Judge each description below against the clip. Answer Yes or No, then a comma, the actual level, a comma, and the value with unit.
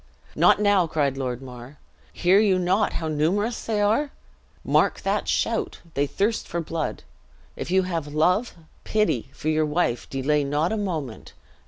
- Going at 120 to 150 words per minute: No, average, 160 wpm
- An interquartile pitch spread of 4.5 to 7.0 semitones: Yes, wide, 5.6 semitones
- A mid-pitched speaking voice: Yes, medium, 165 Hz